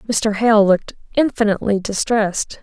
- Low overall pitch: No, high, 215 Hz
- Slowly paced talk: Yes, slow, 115 wpm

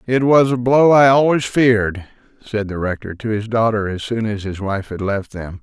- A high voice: No, low, 110 Hz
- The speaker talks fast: Yes, fast, 225 wpm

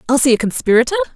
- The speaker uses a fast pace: No, average, 155 wpm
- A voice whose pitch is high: Yes, very high, 280 Hz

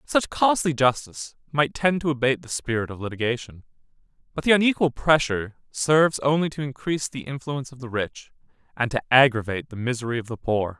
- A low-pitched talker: Yes, low, 130 Hz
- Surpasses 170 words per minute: Yes, average, 180 wpm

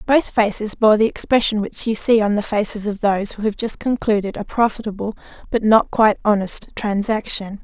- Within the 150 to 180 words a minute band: No, average, 190 wpm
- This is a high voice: Yes, high, 215 Hz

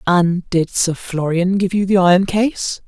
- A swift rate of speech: No, average, 190 wpm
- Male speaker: No, female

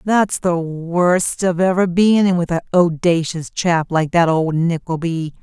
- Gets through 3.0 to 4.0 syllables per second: Yes, 3.9 syllables/s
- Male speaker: No, female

